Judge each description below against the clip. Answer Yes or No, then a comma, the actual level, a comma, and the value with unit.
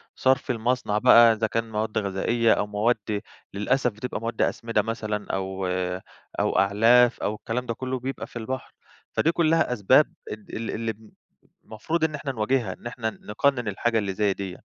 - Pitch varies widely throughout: No, average, 2.9 semitones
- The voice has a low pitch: Yes, low, 115 Hz